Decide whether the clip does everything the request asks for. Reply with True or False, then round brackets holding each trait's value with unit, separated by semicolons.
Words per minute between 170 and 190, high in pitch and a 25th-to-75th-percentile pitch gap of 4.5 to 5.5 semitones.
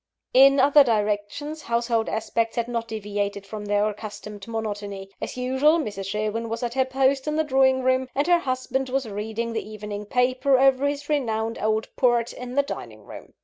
False (185 wpm; 235 Hz; 3.9 semitones)